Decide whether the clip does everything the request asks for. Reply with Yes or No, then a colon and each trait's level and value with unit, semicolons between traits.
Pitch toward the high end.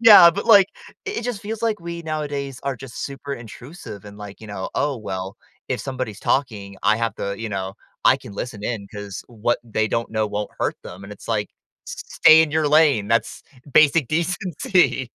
No: low, 125 Hz